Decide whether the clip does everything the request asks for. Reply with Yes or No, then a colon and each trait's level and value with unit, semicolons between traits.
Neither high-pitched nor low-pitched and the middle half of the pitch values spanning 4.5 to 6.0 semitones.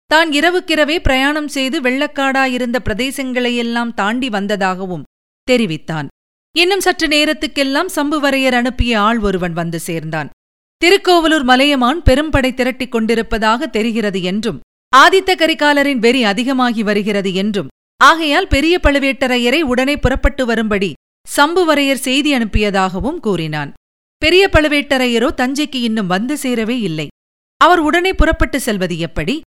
No: very high, 255 Hz; wide, 5.6 semitones